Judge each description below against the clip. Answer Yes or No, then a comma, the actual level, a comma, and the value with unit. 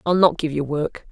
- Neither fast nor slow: No, fast, 270 wpm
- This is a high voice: No, medium, 155 Hz